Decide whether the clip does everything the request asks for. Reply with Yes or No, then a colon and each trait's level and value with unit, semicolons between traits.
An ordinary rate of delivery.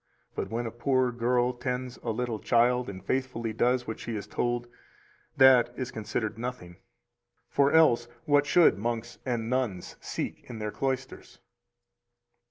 Yes: average, 150 wpm